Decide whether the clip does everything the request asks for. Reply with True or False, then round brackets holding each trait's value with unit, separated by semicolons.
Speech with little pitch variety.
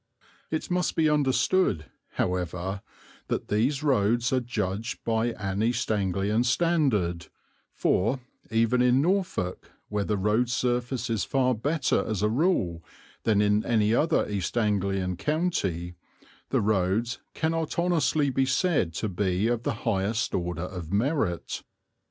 False (5.5 semitones)